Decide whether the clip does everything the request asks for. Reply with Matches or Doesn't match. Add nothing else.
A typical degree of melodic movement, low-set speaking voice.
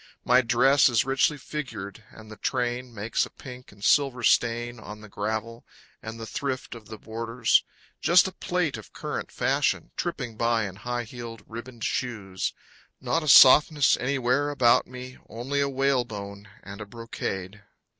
Matches